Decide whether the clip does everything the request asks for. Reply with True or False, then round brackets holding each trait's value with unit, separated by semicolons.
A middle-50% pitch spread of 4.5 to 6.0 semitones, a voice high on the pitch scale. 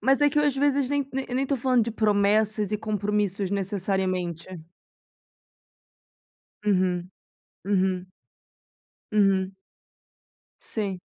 True (4.9 semitones; 210 Hz)